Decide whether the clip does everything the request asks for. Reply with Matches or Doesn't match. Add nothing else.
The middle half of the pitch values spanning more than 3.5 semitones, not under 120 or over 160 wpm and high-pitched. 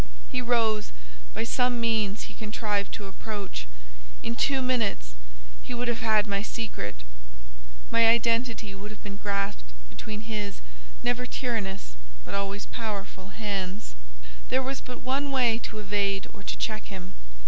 Doesn't match